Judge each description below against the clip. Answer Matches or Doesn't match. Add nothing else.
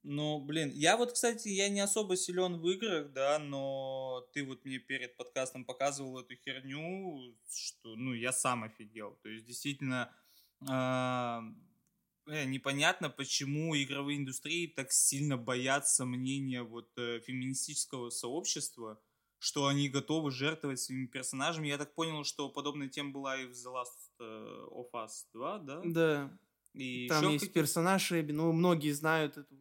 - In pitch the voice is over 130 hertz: Matches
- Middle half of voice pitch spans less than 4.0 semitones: Matches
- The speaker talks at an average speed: Matches